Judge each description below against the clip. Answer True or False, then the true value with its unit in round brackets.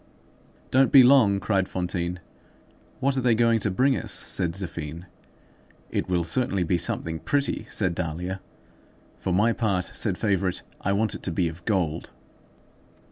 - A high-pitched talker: False (95 Hz)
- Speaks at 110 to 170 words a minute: True (155 wpm)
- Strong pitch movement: False (4.5 semitones)